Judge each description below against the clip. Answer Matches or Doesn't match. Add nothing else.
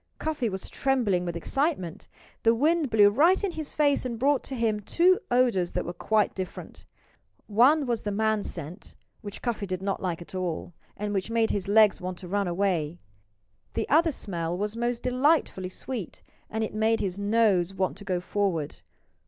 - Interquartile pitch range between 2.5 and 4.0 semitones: Doesn't match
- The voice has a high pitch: Matches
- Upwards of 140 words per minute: Matches